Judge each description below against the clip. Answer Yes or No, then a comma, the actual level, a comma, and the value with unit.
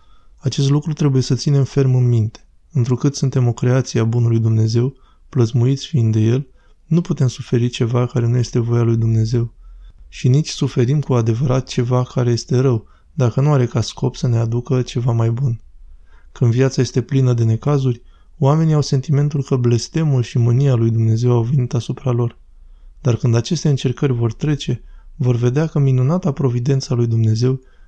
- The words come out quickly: Yes, fast, 175 wpm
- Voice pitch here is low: Yes, low, 125 Hz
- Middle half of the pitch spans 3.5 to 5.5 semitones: No, average, 2.7 semitones